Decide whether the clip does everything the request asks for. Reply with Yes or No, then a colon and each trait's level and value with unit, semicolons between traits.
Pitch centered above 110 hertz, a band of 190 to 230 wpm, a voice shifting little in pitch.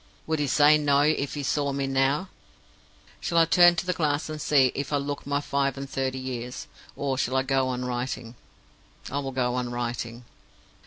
Yes: low, 135 Hz; average, 200 wpm; narrow, 2.2 semitones